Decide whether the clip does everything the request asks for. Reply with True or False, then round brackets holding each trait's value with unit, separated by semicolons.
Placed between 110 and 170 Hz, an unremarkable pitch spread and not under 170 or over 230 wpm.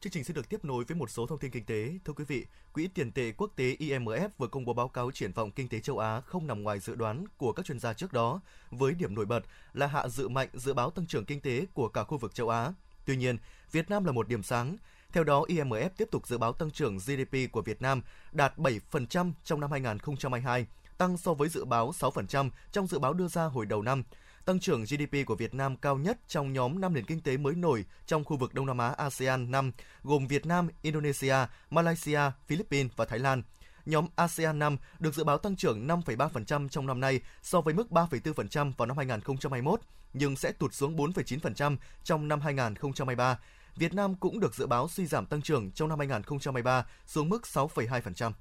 True (140 Hz; 4.2 semitones; 225 wpm)